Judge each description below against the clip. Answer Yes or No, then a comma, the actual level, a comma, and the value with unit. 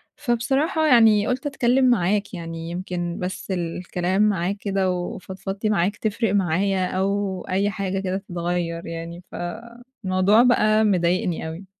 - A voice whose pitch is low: No, high, 190 Hz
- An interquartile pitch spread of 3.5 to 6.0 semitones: No, average, 3.1 semitones